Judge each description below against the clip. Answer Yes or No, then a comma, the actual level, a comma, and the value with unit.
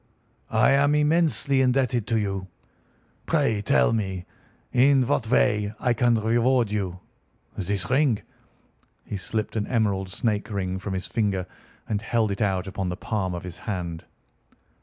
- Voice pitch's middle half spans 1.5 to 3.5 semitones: No, average, 4.4 semitones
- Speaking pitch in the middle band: No, low, 105 Hz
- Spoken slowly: No, average, 150 wpm